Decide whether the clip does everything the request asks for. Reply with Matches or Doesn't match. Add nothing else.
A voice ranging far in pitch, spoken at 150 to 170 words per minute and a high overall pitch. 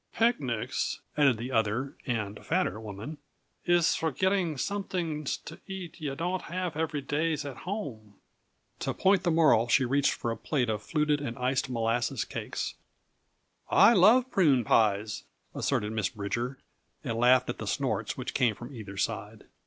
Doesn't match